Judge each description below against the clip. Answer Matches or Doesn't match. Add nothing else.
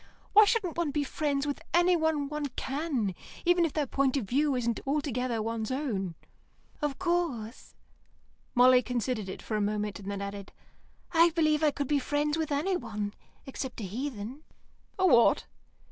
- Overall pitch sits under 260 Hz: Doesn't match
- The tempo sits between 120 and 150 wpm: Doesn't match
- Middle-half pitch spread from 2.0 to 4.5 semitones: Doesn't match